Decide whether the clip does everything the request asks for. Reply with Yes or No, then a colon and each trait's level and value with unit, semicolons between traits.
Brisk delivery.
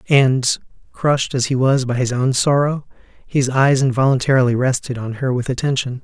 No: average, 170 wpm